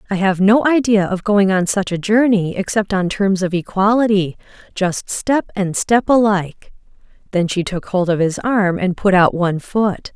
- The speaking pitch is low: No, high, 195 Hz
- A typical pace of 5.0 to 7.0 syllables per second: No, 4.7 syllables/s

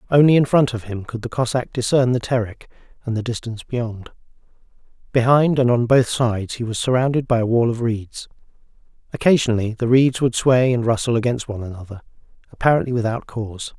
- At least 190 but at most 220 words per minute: No, average, 180 wpm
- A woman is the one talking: No, male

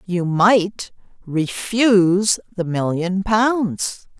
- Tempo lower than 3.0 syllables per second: Yes, 2.5 syllables/s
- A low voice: No, high, 195 Hz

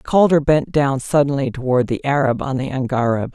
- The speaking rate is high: No, average, 180 wpm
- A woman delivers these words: Yes, female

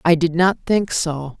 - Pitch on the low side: No, medium, 165 Hz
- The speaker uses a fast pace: Yes, fast, 215 wpm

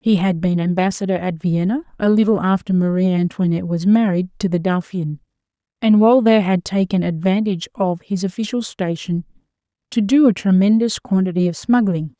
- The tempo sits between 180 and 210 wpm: No, average, 160 wpm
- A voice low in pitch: No, high, 190 Hz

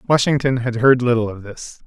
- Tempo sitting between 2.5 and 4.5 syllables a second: No, 5.1 syllables/s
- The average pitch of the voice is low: Yes, low, 125 Hz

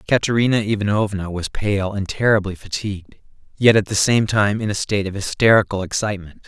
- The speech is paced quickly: No, average, 165 wpm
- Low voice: Yes, low, 100 Hz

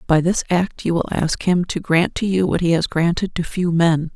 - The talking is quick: Yes, fast, 260 wpm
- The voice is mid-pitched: Yes, medium, 170 Hz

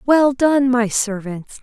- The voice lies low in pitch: No, high, 245 Hz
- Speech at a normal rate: Yes, average, 150 wpm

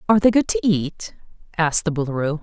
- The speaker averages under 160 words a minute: No, average, 200 wpm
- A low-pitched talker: No, medium, 180 Hz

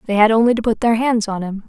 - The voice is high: Yes, high, 220 Hz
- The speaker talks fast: Yes, fast, 320 wpm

